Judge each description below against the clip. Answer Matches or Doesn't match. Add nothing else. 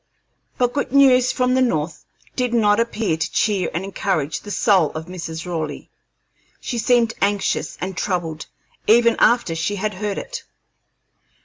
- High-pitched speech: Matches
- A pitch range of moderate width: Doesn't match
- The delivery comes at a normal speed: Matches